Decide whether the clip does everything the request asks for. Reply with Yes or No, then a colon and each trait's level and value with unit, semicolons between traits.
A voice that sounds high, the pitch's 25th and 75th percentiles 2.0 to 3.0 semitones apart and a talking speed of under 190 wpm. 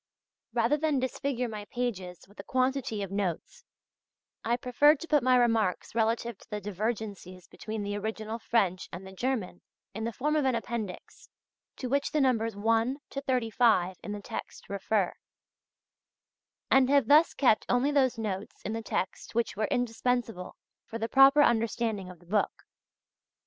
No: high, 225 Hz; average, 3.8 semitones; average, 165 wpm